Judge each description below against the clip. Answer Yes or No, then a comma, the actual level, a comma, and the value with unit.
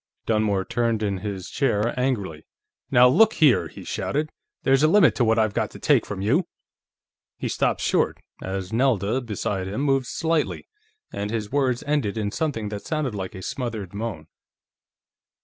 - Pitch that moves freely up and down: No, average, 5.0 semitones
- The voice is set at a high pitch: No, low, 115 Hz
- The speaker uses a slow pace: No, average, 165 wpm